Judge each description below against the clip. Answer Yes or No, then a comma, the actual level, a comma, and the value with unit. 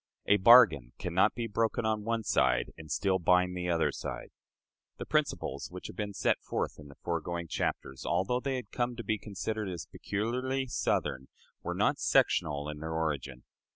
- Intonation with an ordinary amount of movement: No, wide, 6.1 semitones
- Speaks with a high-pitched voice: No, very low, 95 Hz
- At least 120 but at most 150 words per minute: No, average, 185 wpm